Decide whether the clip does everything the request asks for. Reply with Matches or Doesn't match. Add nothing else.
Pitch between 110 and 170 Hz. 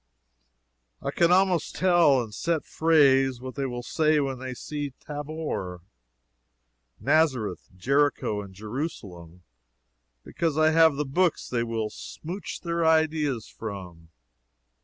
Matches